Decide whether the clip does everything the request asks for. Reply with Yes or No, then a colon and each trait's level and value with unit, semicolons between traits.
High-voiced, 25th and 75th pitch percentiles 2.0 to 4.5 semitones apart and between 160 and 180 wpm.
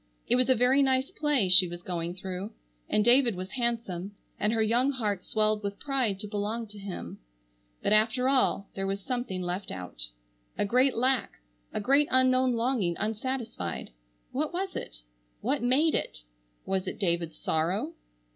No: high, 215 Hz; wide, 5.4 semitones; average, 165 wpm